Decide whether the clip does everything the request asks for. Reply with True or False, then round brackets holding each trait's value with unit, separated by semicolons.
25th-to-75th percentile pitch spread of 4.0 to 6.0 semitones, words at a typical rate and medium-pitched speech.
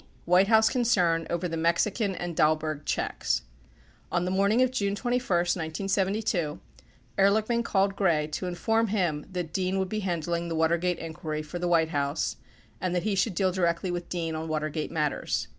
False (3.4 semitones; 180 wpm; 175 Hz)